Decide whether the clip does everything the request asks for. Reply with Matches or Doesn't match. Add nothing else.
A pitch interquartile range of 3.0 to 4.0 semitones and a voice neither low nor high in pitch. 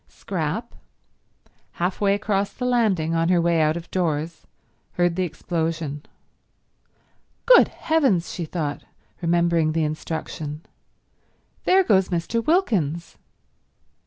Matches